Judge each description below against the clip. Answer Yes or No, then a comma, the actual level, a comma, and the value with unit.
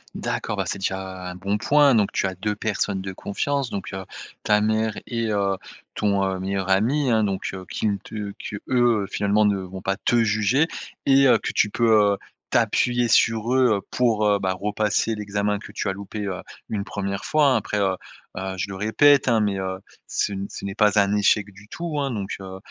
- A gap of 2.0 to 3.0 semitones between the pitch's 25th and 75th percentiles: Yes, narrow, 2.6 semitones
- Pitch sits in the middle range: No, low, 105 Hz